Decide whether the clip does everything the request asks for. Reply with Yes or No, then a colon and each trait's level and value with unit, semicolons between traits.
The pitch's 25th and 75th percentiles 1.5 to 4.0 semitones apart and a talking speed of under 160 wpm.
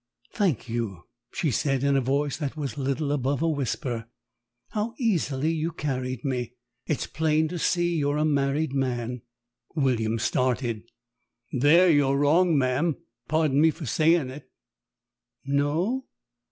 Yes: average, 3.6 semitones; average, 140 wpm